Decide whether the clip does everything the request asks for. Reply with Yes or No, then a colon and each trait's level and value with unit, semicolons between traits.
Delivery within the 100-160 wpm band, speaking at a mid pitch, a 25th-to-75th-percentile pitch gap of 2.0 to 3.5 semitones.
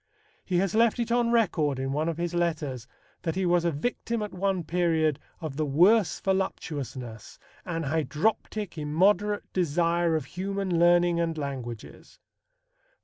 No: average, 145 wpm; medium, 170 Hz; average, 4.1 semitones